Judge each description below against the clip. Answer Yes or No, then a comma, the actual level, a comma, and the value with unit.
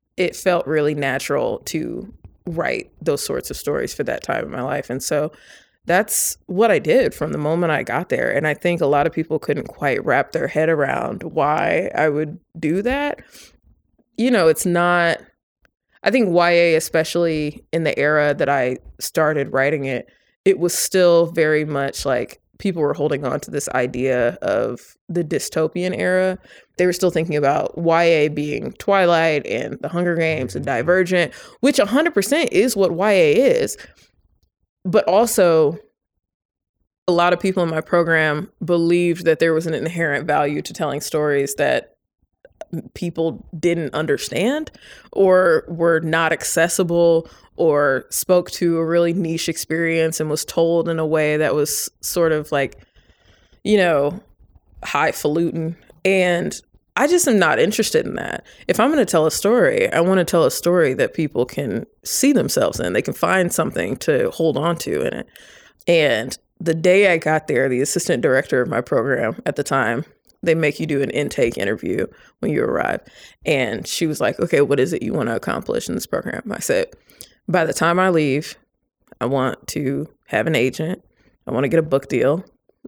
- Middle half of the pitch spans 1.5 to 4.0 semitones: Yes, average, 3.1 semitones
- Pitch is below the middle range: No, medium, 165 Hz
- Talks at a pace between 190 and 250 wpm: No, average, 175 wpm